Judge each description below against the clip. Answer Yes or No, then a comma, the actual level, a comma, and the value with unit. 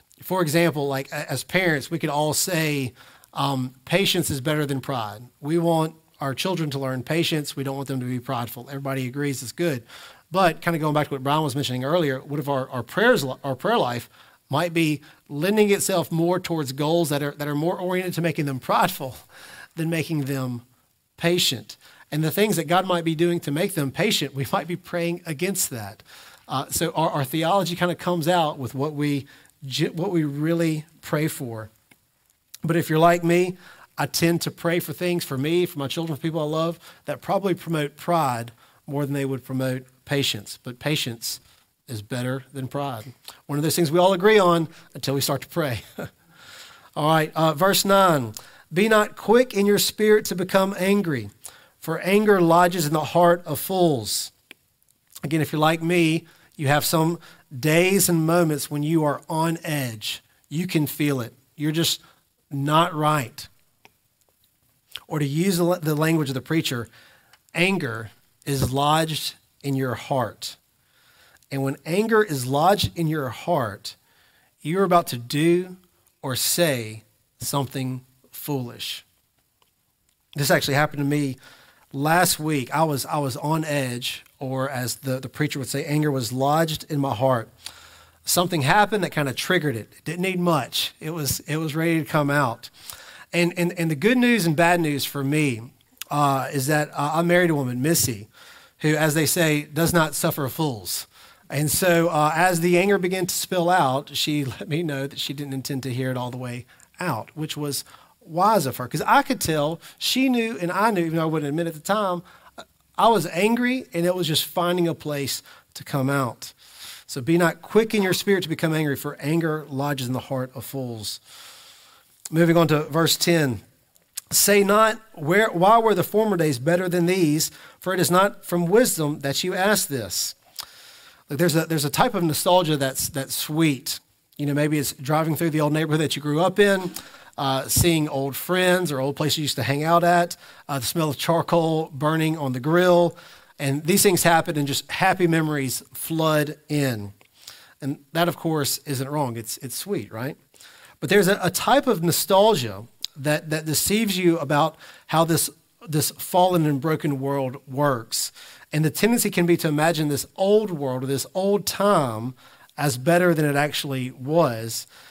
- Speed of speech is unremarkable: Yes, average, 190 wpm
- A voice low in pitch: No, medium, 155 Hz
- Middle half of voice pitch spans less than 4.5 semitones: Yes, average, 4.0 semitones